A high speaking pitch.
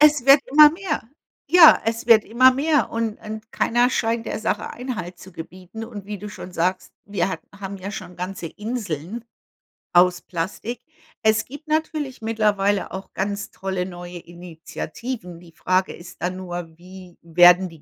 Yes: high, 200 Hz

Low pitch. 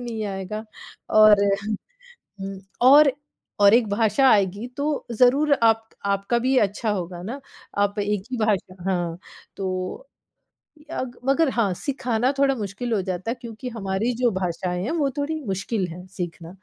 No: high, 215 Hz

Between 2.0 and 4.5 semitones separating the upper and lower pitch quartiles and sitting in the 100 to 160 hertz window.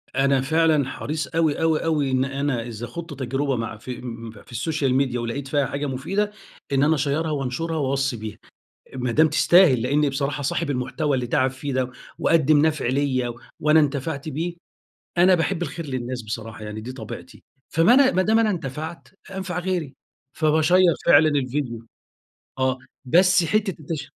Yes: average, 3.9 semitones; medium, 140 Hz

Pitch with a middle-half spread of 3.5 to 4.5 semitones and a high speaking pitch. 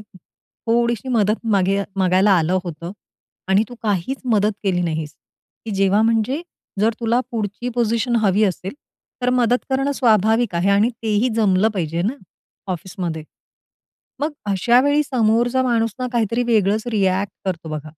Yes: average, 4.0 semitones; high, 215 Hz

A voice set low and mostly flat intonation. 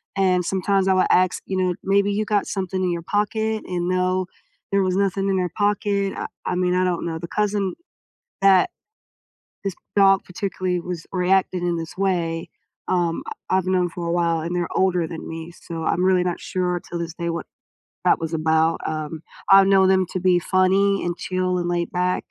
No: medium, 185 Hz; narrow, 1.9 semitones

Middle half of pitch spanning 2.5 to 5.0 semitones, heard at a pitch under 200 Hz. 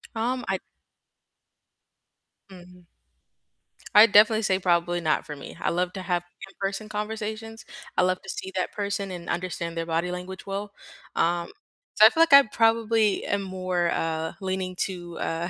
Yes: average, 3.3 semitones; high, 190 Hz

